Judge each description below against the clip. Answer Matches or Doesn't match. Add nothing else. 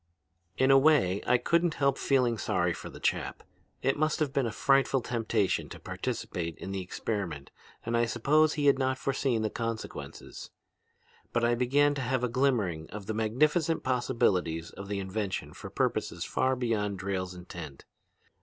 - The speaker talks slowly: Doesn't match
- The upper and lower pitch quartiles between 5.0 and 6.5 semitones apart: Matches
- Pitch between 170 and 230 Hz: Doesn't match